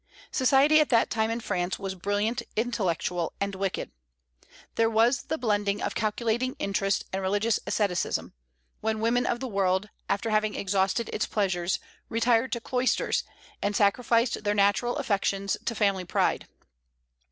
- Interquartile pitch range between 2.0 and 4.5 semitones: Yes, average, 2.9 semitones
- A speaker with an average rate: Yes, average, 145 wpm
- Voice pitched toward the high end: Yes, high, 215 Hz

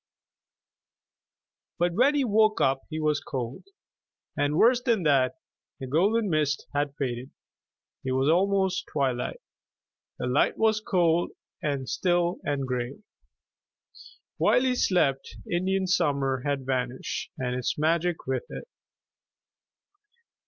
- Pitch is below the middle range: No, medium, 155 Hz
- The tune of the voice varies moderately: No, wide, 6.0 semitones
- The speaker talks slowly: Yes, slow, 115 wpm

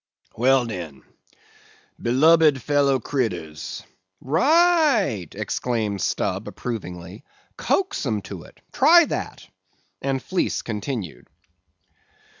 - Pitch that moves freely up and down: Yes, wide, 7.9 semitones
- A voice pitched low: Yes, low, 130 Hz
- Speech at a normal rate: No, slow, 85 wpm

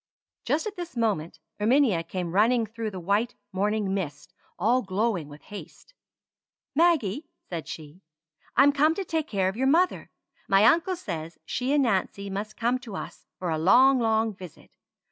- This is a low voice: No, high, 220 Hz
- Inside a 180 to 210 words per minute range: No, average, 165 wpm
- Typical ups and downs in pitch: No, wide, 6.1 semitones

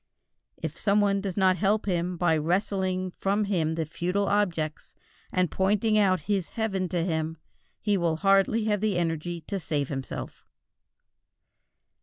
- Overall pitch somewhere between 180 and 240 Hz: Yes, medium, 185 Hz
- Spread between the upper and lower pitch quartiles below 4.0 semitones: Yes, average, 3.3 semitones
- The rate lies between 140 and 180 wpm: Yes, average, 150 wpm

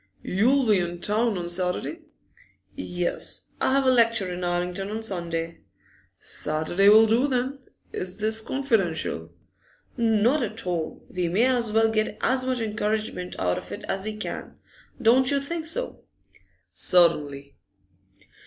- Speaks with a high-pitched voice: Yes, high, 215 Hz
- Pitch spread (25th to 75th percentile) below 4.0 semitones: No, average, 5.1 semitones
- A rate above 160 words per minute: No, average, 145 wpm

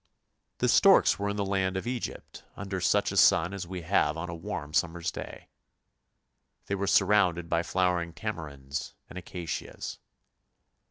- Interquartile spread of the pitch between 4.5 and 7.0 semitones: No, average, 2.9 semitones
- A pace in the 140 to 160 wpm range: Yes, average, 155 wpm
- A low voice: Yes, very low, 90 Hz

